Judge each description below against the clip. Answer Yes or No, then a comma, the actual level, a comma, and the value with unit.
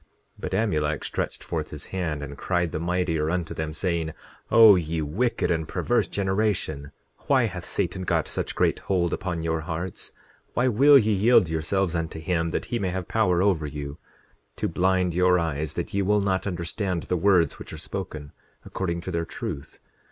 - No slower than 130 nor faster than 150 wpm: No, average, 185 wpm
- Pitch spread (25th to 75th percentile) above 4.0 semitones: No, average, 3.1 semitones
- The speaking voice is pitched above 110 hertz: No, very low, 90 Hz